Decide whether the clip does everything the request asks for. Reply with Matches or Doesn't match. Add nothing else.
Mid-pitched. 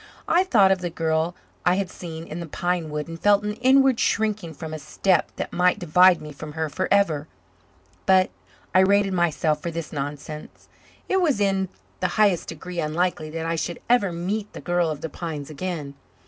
Matches